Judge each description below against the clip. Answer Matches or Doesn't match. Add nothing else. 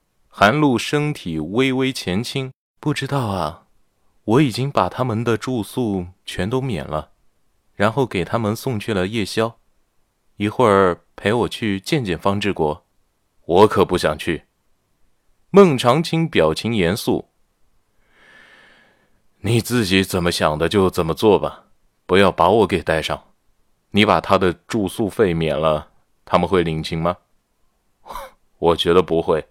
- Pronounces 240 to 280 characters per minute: Doesn't match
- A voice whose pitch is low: Matches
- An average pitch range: Doesn't match